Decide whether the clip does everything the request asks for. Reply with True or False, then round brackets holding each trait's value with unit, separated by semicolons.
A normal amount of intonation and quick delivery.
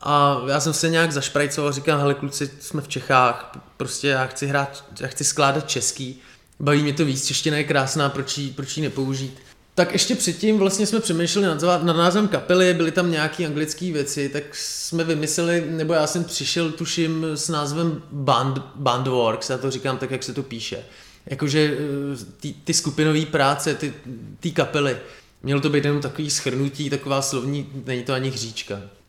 True (3.0 semitones; 180 wpm)